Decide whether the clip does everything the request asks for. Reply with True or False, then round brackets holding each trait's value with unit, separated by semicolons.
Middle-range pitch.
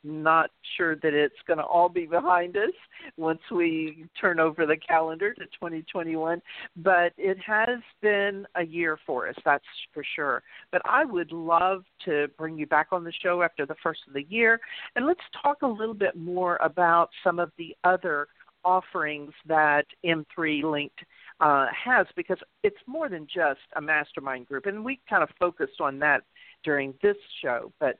True (170 Hz)